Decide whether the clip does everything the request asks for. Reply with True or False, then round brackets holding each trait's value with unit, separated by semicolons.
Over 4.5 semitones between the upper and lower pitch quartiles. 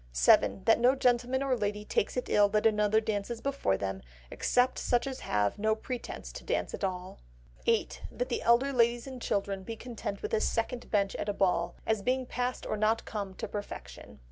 False (3.4 semitones)